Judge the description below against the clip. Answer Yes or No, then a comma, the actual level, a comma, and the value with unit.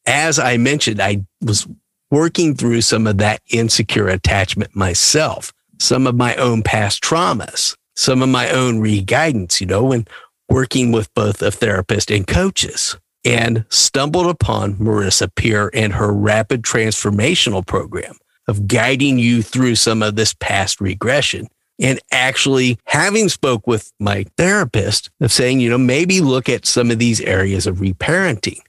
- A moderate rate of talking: Yes, average, 155 wpm